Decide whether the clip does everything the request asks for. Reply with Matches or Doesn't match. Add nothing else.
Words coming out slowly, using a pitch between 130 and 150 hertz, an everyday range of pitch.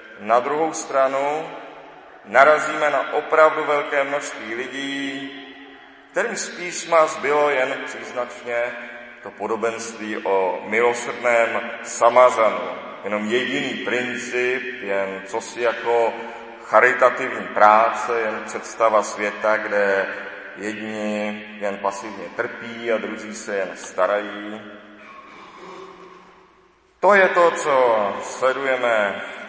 Doesn't match